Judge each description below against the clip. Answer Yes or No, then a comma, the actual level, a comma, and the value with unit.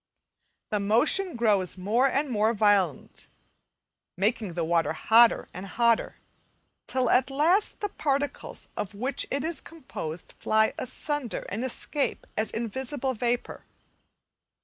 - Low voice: No, high, 235 Hz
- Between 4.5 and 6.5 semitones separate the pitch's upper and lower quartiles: Yes, average, 4.8 semitones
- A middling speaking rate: No, slow, 125 wpm